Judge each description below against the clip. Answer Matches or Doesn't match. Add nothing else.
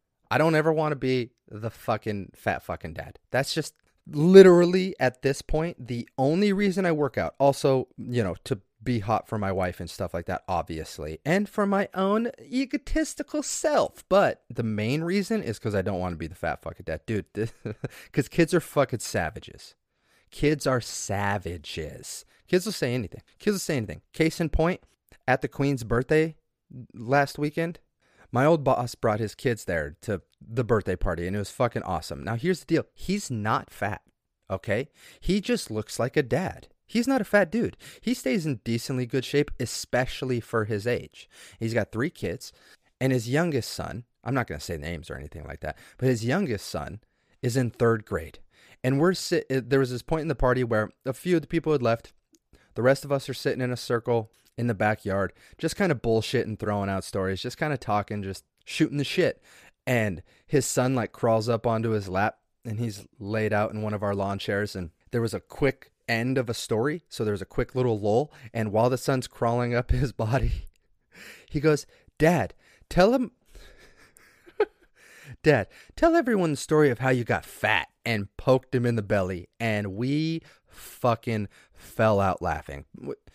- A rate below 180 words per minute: Doesn't match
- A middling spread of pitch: Doesn't match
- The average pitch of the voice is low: Matches